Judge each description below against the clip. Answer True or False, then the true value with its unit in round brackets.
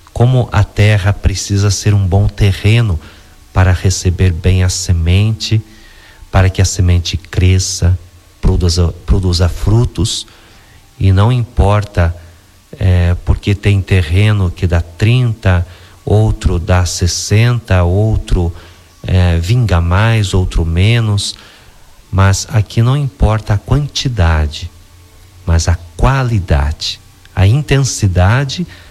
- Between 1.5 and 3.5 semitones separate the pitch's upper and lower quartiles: True (3.0 semitones)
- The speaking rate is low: True (105 wpm)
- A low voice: True (95 Hz)